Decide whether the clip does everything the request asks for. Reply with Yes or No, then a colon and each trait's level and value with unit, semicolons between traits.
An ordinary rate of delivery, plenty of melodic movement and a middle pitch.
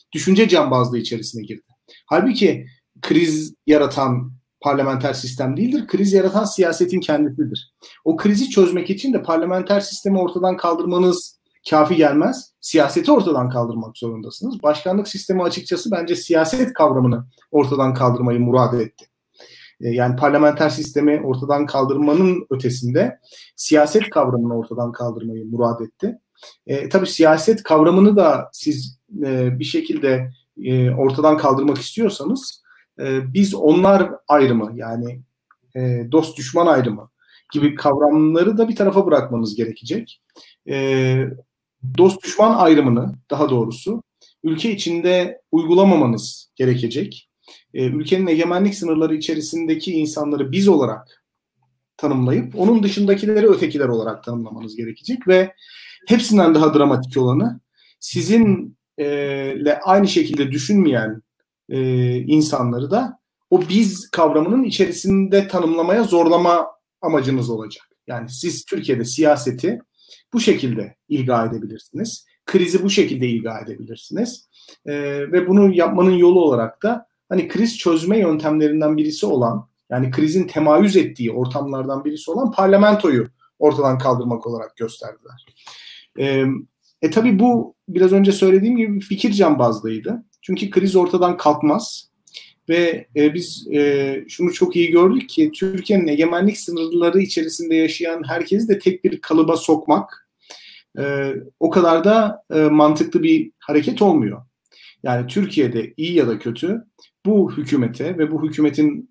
Yes: average, 120 wpm; wide, 6.6 semitones; medium, 155 Hz